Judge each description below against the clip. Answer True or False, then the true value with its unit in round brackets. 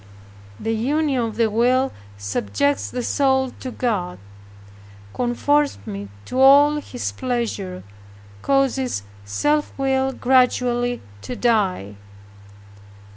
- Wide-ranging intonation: False (4.0 semitones)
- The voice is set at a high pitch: True (245 Hz)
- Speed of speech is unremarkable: False (100 wpm)